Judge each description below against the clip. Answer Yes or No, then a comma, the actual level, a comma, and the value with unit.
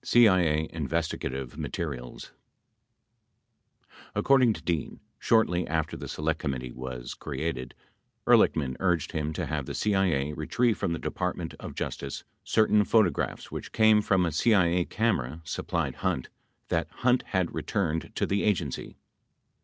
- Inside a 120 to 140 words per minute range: Yes, slow, 135 wpm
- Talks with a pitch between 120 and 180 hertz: No, very low, 85 Hz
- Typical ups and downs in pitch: No, wide, 5.7 semitones